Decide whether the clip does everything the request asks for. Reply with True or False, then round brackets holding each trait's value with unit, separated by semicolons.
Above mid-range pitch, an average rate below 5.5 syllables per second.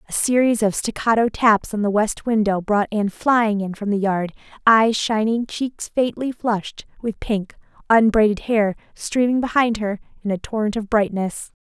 True (215 Hz; 4.6 syllables/s)